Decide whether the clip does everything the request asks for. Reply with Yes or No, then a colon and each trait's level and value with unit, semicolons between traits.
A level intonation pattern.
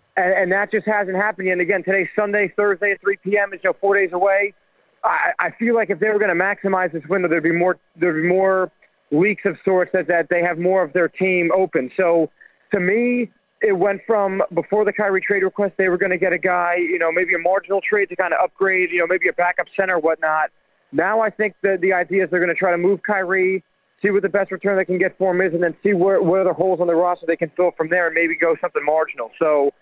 Yes: narrow, 2.2 semitones